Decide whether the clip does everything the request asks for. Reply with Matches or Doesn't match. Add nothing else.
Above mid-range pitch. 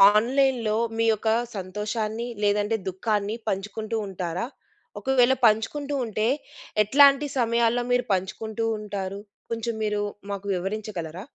Matches